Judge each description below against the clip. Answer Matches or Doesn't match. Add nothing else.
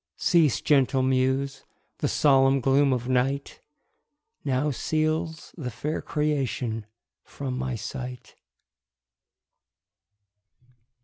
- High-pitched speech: Doesn't match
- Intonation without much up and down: Matches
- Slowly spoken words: Matches